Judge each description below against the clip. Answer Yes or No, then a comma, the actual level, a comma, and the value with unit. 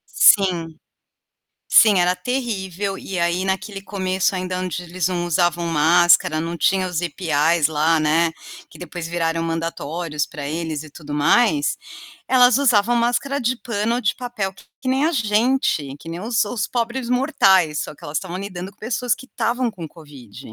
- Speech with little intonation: No, wide, 5.4 semitones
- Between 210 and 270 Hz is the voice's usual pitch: No, medium, 185 Hz